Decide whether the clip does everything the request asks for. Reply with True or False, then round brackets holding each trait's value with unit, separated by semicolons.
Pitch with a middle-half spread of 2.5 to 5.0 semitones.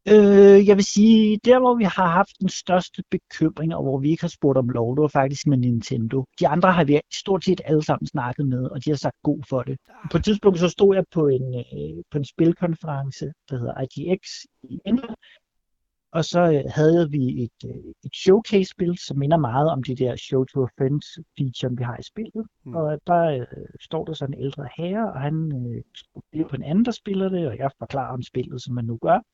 False (5.6 semitones)